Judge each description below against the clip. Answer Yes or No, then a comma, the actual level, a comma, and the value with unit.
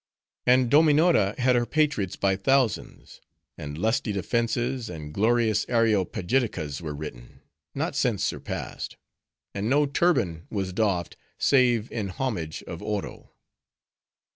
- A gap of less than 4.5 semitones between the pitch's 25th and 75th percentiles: No, wide, 5.5 semitones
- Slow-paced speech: Yes, slow, 115 wpm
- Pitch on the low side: Yes, low, 110 Hz